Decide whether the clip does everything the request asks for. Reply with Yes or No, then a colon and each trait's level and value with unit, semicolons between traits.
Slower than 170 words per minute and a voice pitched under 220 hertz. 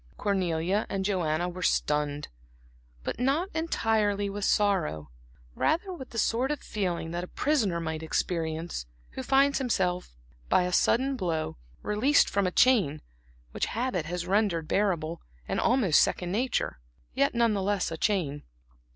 Yes: average, 150 wpm; high, 190 Hz